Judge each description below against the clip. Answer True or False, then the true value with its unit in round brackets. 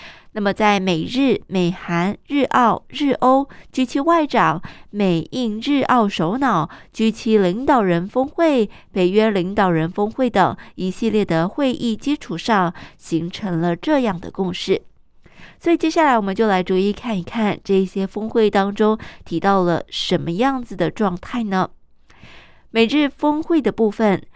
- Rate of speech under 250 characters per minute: True (225 characters per minute)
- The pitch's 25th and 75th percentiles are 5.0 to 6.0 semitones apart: True (5.5 semitones)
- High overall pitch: True (210 Hz)